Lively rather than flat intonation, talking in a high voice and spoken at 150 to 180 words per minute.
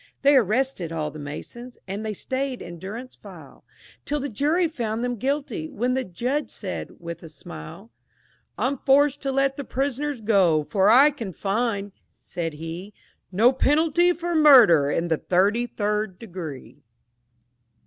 Yes: wide, 7.1 semitones; high, 230 Hz; average, 155 wpm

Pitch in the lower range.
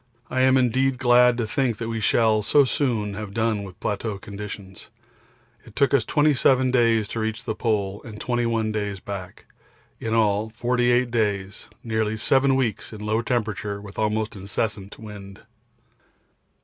Yes: low, 110 Hz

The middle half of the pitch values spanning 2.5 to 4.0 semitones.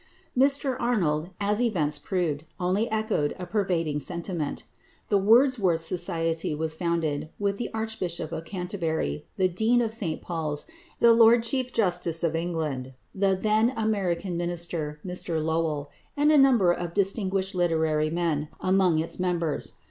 No: average, 4.6 semitones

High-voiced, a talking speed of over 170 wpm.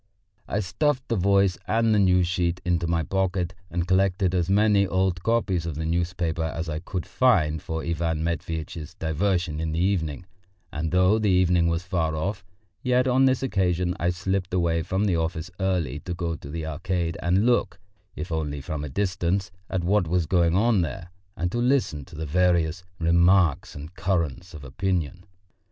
No: very low, 90 Hz; average, 180 wpm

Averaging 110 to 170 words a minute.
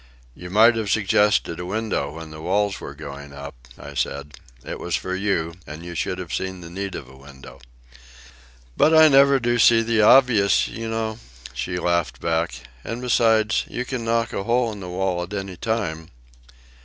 No: average, 190 wpm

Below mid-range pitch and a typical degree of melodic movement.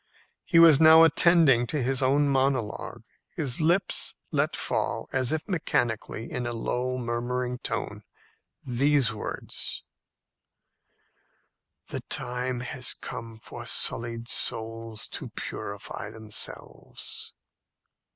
Yes: low, 125 Hz; average, 3.7 semitones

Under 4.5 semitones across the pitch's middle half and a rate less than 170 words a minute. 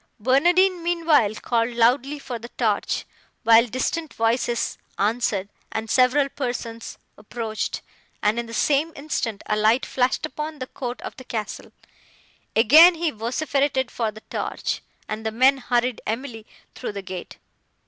Yes: average, 3.8 semitones; average, 145 wpm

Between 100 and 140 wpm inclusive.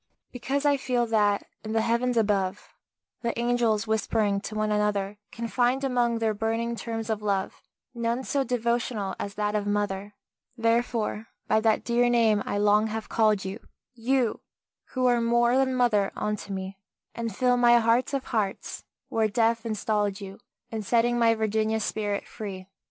No: average, 165 wpm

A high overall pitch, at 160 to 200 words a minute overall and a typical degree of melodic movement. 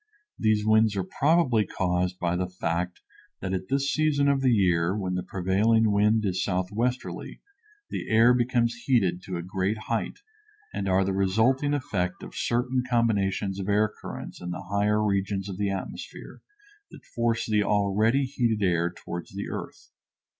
No: low, 105 Hz; average, 165 wpm; average, 3.9 semitones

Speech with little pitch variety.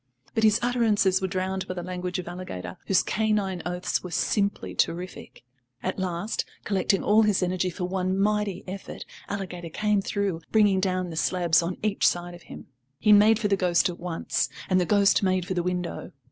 Yes: narrow, 2.2 semitones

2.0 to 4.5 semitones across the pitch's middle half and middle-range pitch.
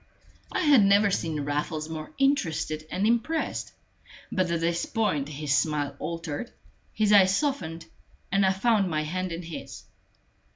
No: average, 5.0 semitones; medium, 170 Hz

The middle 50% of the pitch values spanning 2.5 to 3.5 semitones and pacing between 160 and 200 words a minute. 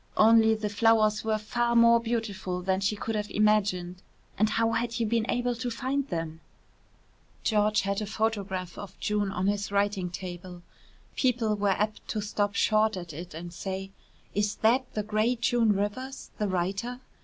Yes: average, 2.8 semitones; average, 170 wpm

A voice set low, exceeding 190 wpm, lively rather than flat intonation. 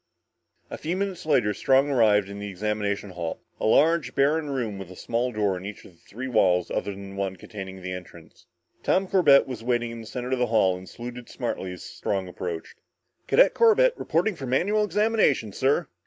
Yes: low, 115 Hz; average, 200 wpm; wide, 6.7 semitones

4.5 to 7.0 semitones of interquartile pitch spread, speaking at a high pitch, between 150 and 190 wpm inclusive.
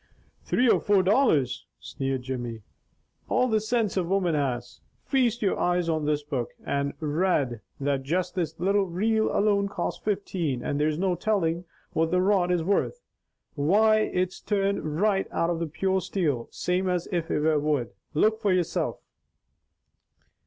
No: average, 5.0 semitones; medium, 180 Hz; average, 160 wpm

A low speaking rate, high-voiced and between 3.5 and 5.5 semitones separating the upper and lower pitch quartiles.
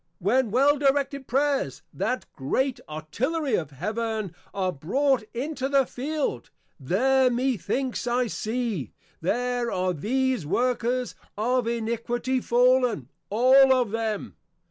Yes: slow, 115 wpm; high, 245 Hz; average, 3.9 semitones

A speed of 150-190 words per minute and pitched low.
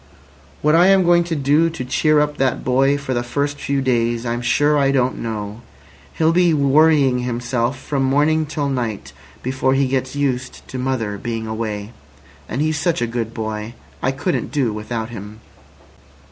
Yes: average, 175 wpm; low, 130 Hz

